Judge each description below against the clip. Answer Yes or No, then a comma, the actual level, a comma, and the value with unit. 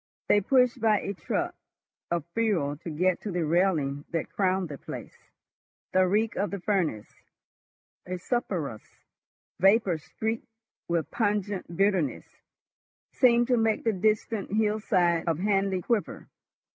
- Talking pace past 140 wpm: No, slow, 135 wpm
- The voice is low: No, high, 195 Hz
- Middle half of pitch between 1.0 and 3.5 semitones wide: No, average, 4.0 semitones